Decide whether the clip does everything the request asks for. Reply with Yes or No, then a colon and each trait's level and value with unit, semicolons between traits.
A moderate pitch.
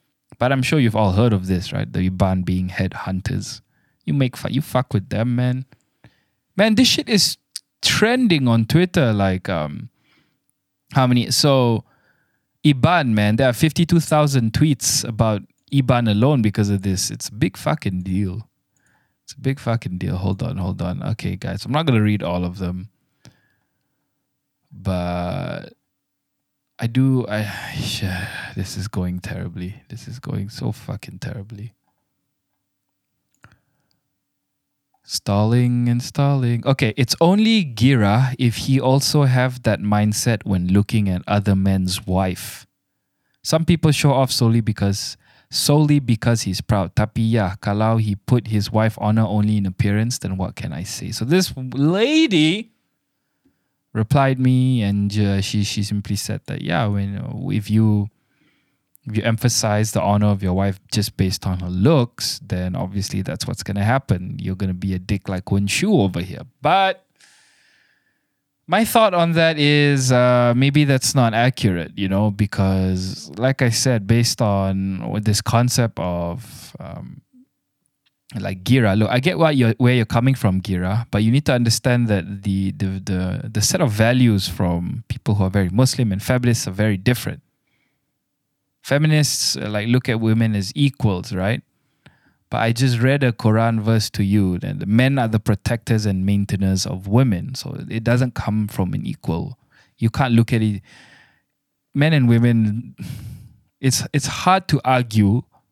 No: low, 115 Hz